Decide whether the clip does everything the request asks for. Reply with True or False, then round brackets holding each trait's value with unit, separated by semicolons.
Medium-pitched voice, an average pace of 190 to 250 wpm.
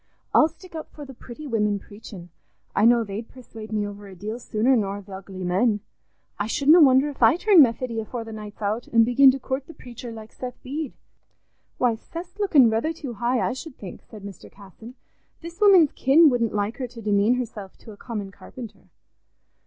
False (235 Hz; 200 wpm)